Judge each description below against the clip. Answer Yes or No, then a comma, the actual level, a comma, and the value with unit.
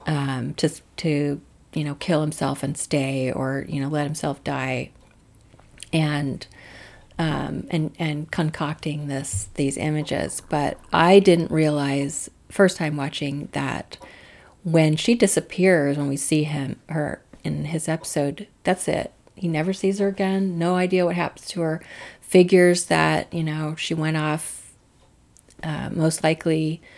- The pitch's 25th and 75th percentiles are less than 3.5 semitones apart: Yes, average, 3.0 semitones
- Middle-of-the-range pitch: Yes, medium, 155 Hz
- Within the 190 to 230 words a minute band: No, average, 145 wpm